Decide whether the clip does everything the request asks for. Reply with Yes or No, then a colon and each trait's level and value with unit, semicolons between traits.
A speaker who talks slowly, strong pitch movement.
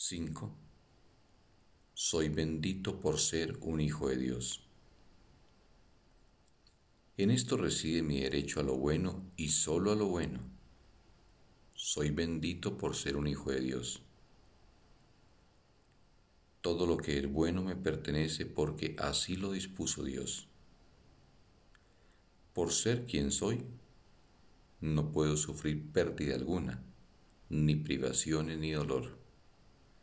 No: slow, 110 wpm; average, 3.8 semitones